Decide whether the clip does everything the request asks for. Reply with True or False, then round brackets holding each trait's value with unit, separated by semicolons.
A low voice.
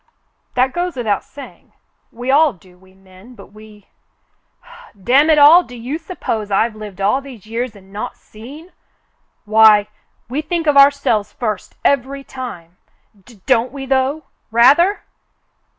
False (245 Hz)